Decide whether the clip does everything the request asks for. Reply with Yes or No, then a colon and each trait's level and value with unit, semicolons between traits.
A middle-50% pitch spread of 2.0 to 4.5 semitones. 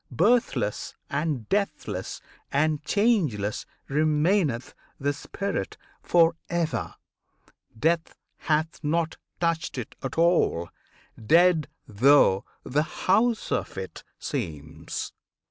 No: average, 5.3 semitones